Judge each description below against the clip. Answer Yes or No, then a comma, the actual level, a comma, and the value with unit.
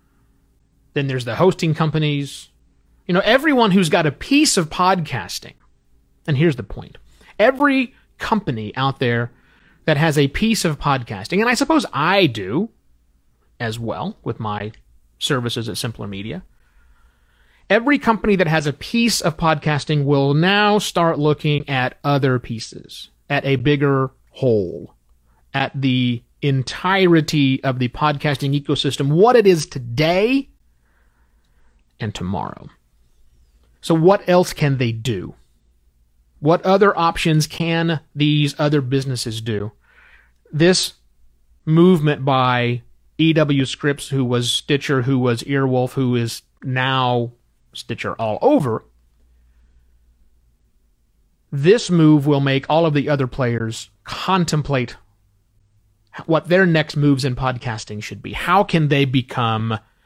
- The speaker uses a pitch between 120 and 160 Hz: Yes, low, 135 Hz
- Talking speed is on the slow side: Yes, slow, 125 wpm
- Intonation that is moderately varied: No, wide, 7.0 semitones